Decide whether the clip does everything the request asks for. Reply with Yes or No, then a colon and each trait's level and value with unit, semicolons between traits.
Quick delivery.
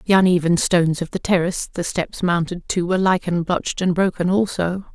No: average, 195 wpm